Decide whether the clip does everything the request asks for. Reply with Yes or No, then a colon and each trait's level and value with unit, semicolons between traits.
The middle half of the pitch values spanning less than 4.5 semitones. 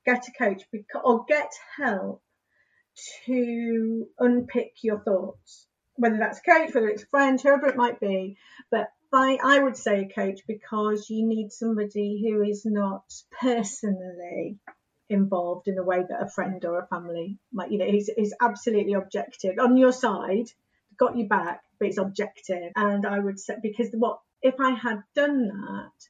Yes: average, 3.6 semitones